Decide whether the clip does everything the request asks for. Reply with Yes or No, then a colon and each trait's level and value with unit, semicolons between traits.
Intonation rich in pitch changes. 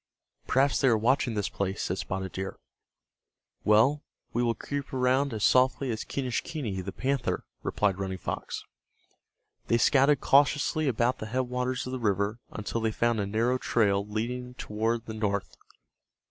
No: average, 3.7 semitones